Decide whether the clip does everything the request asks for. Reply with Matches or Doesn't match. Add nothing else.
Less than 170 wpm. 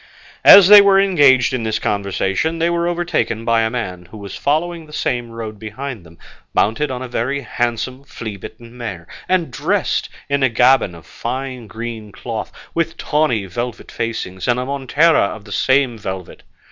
Doesn't match